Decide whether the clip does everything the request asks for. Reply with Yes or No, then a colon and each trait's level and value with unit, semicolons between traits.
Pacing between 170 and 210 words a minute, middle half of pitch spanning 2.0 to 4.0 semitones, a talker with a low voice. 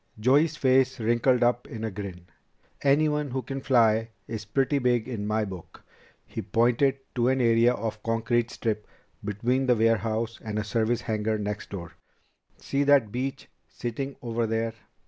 No: average, 160 wpm; average, 3.1 semitones; low, 115 Hz